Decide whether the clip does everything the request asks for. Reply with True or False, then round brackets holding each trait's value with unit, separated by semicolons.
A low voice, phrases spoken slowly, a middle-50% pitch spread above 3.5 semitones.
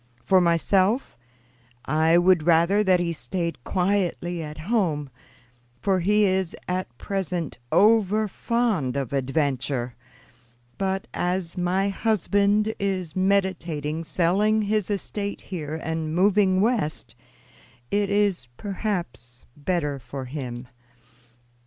False (180 Hz; 110 wpm; 4.4 semitones)